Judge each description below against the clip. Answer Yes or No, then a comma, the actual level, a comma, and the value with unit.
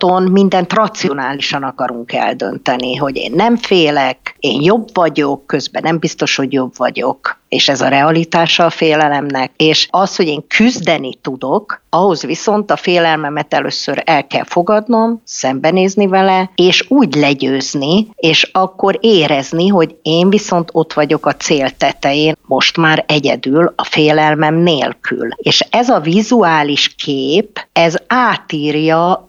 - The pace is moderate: Yes, average, 135 wpm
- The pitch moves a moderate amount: Yes, average, 4.3 semitones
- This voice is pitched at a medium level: Yes, medium, 165 Hz